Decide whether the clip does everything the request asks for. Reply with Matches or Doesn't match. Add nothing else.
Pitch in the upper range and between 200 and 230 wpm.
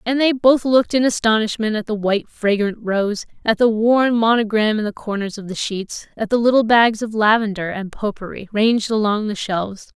Matches